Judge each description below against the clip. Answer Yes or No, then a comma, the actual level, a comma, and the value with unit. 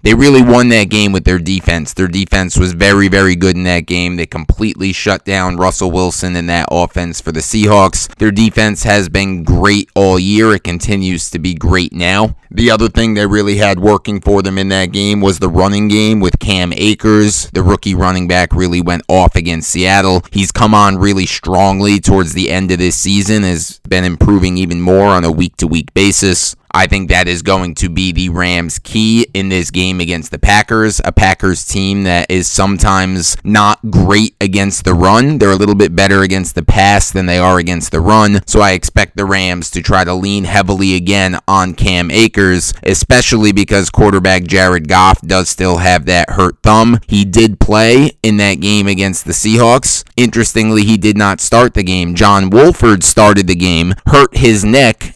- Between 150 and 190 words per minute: No, average, 200 wpm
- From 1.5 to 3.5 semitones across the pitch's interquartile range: Yes, narrow, 2.4 semitones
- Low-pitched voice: Yes, very low, 95 Hz